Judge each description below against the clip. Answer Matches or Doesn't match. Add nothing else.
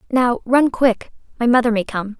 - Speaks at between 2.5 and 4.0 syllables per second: Doesn't match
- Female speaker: Matches